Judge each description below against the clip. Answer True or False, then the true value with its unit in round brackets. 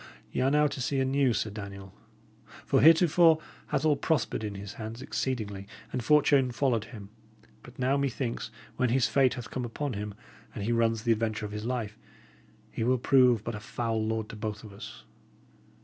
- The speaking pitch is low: True (115 Hz)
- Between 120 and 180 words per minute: False (195 wpm)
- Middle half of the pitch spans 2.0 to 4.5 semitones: True (3.8 semitones)